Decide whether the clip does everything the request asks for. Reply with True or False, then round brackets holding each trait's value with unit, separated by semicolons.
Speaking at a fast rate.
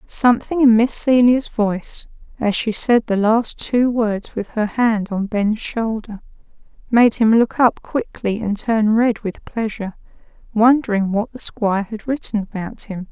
False (165 wpm)